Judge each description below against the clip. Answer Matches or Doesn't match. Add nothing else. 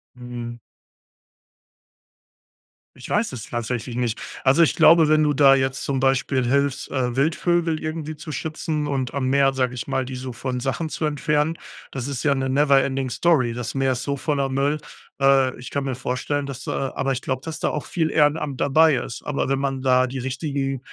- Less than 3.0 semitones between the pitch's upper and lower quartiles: Matches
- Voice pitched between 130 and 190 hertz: Matches